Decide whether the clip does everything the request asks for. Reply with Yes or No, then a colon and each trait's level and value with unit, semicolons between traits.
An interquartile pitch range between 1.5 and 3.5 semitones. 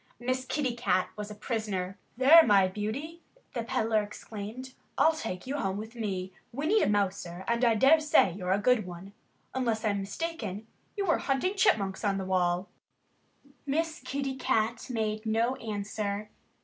No: average, 4.7 semitones